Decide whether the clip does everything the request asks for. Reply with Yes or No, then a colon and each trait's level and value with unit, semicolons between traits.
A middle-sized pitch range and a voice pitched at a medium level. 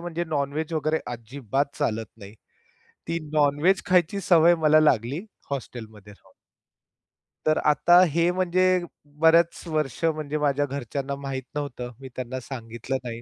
Yes: average, 4.4 semitones; medium, 145 Hz